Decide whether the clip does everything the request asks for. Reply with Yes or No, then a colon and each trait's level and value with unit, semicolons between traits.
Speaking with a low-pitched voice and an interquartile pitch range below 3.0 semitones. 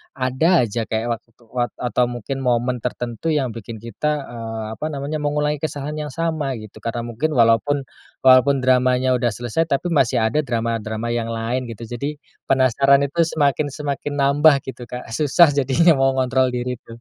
No: low, 130 Hz; average, 3.5 semitones